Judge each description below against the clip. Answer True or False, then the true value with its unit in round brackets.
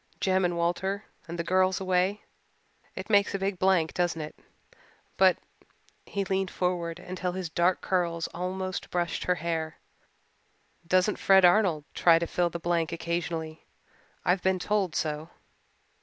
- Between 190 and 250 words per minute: False (150 wpm)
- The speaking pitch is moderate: True (180 Hz)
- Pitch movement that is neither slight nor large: False (1.9 semitones)